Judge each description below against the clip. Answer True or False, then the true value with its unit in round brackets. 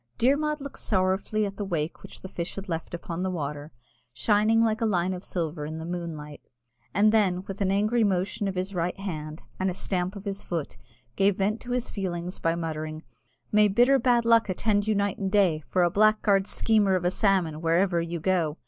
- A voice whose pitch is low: False (190 Hz)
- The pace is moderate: False (210 wpm)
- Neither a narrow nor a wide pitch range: True (3.6 semitones)